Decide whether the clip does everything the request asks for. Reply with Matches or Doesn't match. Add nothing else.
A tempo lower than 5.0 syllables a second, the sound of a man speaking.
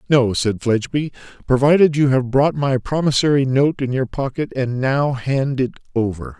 Matches